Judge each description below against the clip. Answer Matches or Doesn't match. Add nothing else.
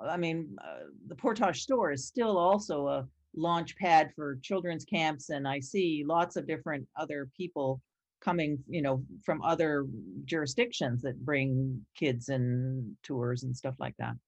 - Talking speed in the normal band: Matches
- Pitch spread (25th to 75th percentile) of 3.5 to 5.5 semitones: Matches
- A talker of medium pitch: Matches